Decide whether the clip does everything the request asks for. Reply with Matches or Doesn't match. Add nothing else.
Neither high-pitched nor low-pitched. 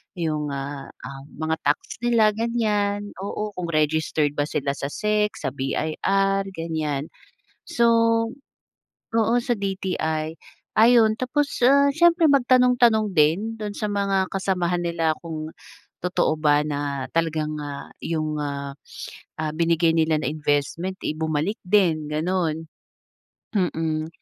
Matches